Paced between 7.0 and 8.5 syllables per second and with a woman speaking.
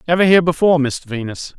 No: 7.3 syllables/s; male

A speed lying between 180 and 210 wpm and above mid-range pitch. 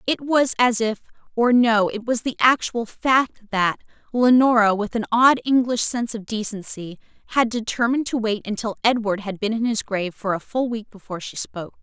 Yes: average, 185 wpm; high, 225 Hz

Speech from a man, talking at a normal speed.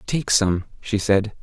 Yes: male; average, 170 wpm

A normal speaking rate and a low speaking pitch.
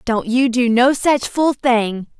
No: average, 190 wpm; high, 245 Hz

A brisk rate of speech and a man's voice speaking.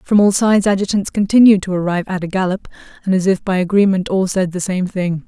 No: fast, 230 wpm; female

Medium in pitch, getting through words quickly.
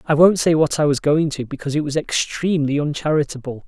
Yes: medium, 150 Hz; fast, 210 wpm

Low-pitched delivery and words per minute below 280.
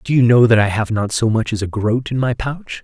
No: low, 115 Hz; fast, 320 wpm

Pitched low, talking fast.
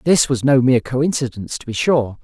Yes: low, 130 Hz; fast, 215 wpm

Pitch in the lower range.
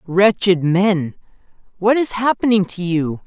No: high, 190 Hz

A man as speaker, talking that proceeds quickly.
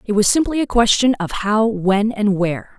No: female; fast, 215 wpm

